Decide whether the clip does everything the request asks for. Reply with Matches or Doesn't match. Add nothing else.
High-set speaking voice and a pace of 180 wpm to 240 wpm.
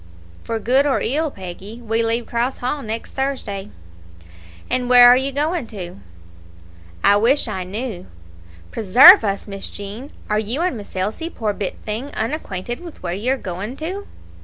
Doesn't match